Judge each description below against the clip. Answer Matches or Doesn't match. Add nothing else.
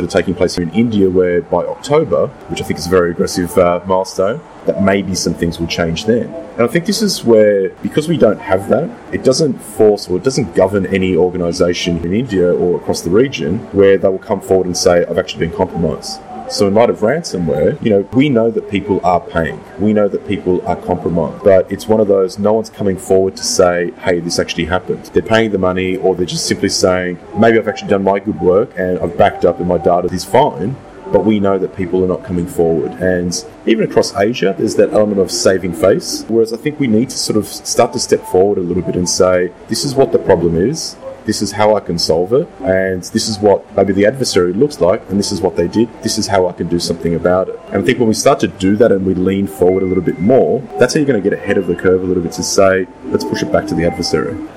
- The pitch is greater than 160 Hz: Doesn't match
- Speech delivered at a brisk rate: Matches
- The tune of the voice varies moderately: Matches